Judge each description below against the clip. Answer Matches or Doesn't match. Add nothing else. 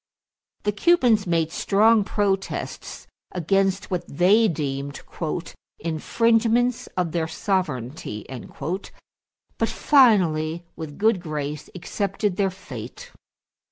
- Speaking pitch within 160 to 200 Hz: Matches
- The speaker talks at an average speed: Doesn't match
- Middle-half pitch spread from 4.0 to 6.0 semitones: Matches